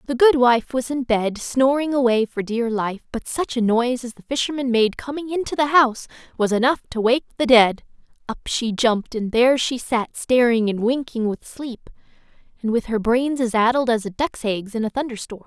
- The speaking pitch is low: No, high, 240 Hz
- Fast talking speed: Yes, fast, 215 wpm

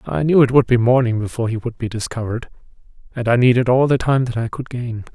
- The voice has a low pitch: Yes, low, 120 Hz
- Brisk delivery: Yes, fast, 245 wpm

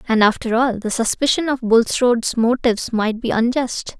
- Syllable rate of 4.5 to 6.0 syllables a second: Yes, 5.0 syllables/s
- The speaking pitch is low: No, high, 235 Hz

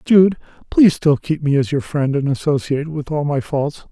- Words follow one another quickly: Yes, fast, 215 wpm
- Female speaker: No, male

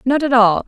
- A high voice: Yes, high, 245 Hz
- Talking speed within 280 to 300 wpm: No, fast, 265 wpm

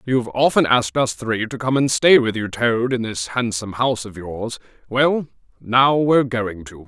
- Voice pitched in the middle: No, low, 120 Hz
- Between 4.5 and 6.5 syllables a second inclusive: Yes, 5.0 syllables/s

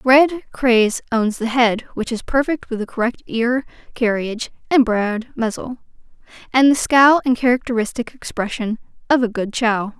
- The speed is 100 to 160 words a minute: Yes, average, 155 wpm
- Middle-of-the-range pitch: No, high, 240 Hz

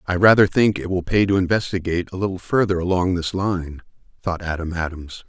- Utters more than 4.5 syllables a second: Yes, 5.8 syllables/s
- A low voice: Yes, very low, 90 Hz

